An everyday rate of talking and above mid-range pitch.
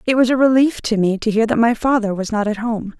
No: fast, 300 wpm; high, 225 Hz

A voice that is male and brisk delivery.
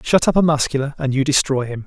Yes: male; fast, 255 wpm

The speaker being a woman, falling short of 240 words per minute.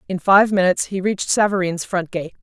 Yes: female; average, 200 wpm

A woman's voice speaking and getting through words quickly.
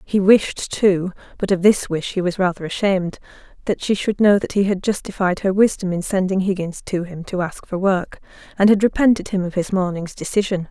Yes: female; fast, 215 wpm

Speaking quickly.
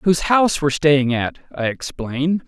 No: average, 170 wpm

